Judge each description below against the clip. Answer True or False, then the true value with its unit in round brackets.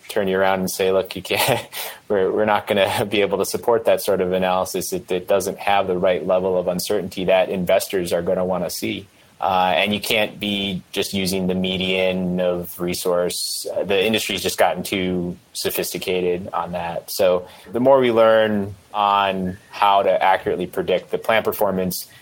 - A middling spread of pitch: False (1.6 semitones)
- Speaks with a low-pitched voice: True (95 Hz)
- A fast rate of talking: False (190 wpm)